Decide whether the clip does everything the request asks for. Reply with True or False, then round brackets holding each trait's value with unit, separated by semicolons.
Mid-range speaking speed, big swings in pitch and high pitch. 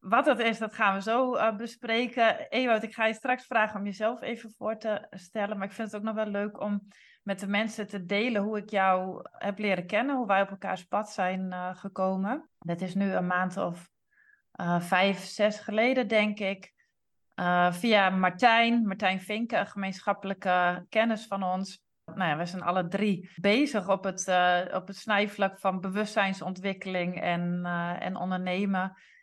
False (185 wpm; 2.9 semitones; 200 Hz)